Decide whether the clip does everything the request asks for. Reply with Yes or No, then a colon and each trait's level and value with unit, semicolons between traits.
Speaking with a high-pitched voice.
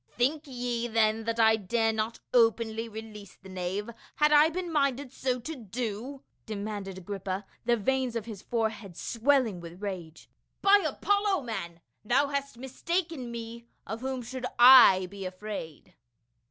Yes: high, 230 Hz